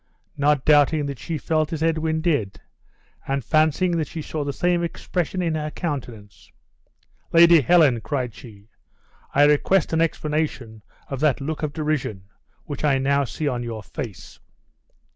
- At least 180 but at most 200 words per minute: No, average, 155 wpm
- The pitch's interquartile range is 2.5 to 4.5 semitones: Yes, average, 3.2 semitones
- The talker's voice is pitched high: No, medium, 150 Hz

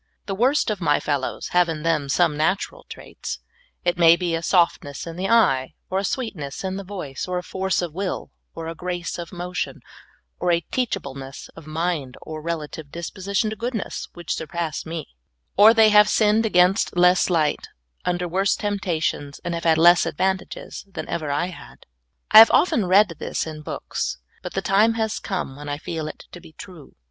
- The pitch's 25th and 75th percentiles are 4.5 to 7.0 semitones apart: No, average, 3.6 semitones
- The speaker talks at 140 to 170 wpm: No, average, 195 wpm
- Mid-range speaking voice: Yes, medium, 175 Hz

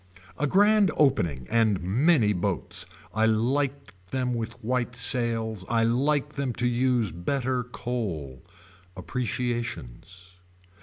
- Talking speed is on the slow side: Yes, slow, 110 wpm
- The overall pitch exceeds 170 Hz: No, low, 120 Hz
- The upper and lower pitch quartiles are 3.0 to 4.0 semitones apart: Yes, average, 3.6 semitones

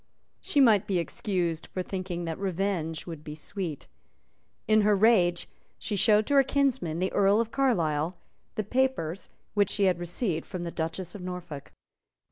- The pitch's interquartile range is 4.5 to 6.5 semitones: No, average, 3.8 semitones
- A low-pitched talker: No, medium, 185 Hz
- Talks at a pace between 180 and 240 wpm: No, average, 165 wpm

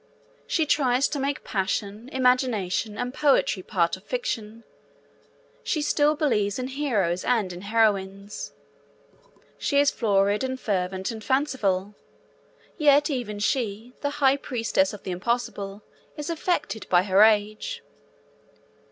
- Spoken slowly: Yes, slow, 125 wpm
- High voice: Yes, high, 225 Hz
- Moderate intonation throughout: No, wide, 5.7 semitones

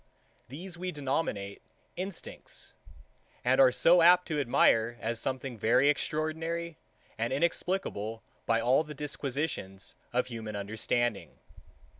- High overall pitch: No, low, 135 Hz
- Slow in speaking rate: Yes, slow, 115 wpm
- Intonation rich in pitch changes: Yes, wide, 6.0 semitones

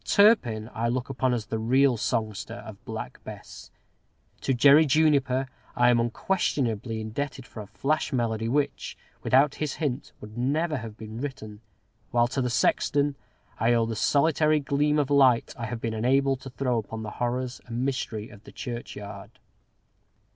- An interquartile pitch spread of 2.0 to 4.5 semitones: Yes, average, 3.7 semitones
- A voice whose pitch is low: Yes, low, 125 Hz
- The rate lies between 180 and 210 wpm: No, average, 165 wpm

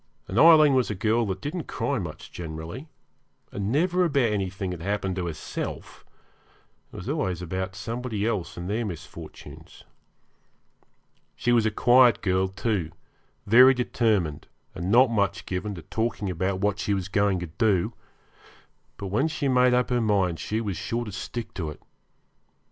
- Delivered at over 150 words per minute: Yes, average, 165 wpm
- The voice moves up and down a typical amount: Yes, average, 4.5 semitones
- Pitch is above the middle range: No, low, 105 Hz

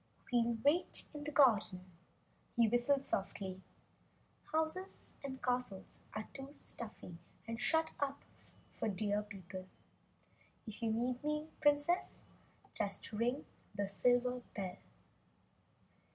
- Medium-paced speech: No, slow, 110 wpm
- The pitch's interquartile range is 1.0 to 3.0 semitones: No, wide, 5.6 semitones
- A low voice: No, high, 240 Hz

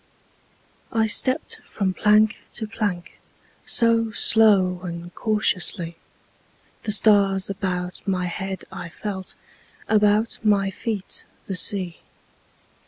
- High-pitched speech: Yes, high, 200 Hz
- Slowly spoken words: Yes, slow, 105 wpm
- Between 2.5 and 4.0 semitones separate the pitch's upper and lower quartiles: Yes, average, 2.8 semitones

